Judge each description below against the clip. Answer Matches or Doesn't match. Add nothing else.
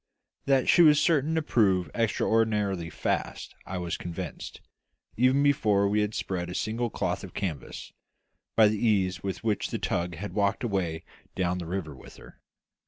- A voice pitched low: Matches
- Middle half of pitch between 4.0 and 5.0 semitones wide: Matches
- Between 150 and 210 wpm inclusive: Matches